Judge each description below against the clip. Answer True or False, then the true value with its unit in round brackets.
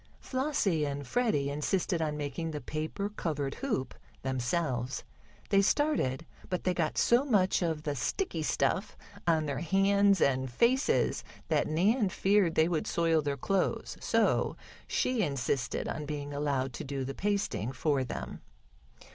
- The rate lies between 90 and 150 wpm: True (145 wpm)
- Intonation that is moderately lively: False (5.8 semitones)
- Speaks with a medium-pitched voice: True (160 Hz)